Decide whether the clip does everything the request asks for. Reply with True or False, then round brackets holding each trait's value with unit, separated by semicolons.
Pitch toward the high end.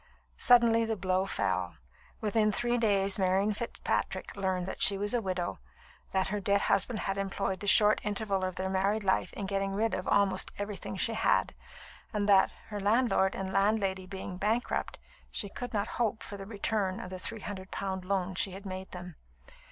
True (195 Hz)